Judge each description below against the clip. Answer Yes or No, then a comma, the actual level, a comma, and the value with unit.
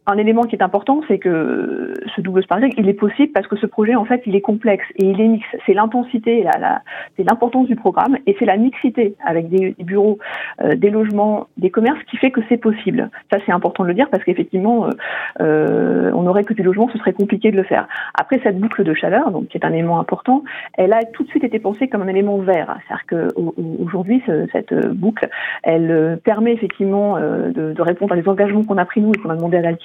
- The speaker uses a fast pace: Yes, fast, 245 wpm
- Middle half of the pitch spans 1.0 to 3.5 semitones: No, average, 4.0 semitones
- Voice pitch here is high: Yes, high, 210 Hz